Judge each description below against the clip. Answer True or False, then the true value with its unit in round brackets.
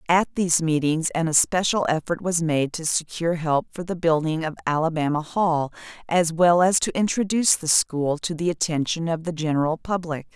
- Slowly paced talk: False (180 wpm)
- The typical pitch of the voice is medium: True (165 Hz)